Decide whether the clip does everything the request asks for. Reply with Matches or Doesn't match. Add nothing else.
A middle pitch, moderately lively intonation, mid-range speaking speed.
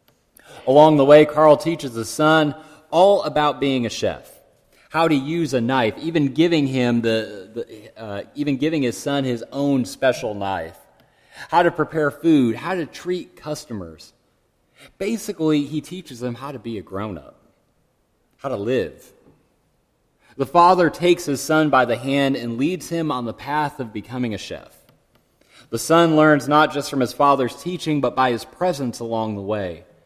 Matches